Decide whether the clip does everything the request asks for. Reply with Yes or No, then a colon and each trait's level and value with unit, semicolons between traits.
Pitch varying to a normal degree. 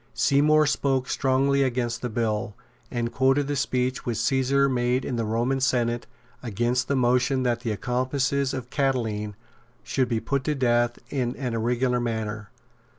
No: narrow, 2.2 semitones